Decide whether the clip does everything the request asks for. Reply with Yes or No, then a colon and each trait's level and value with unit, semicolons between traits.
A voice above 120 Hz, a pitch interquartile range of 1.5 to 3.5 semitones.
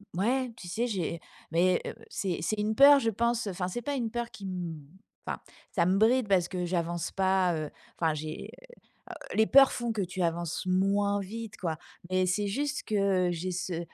No: high, 190 Hz; average, 4.1 semitones